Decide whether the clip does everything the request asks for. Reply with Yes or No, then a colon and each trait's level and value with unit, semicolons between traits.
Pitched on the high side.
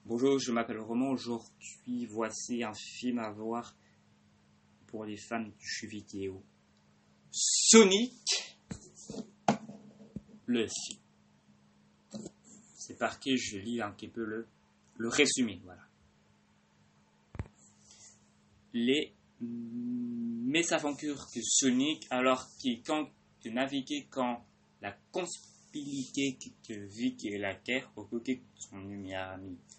No: low, 120 Hz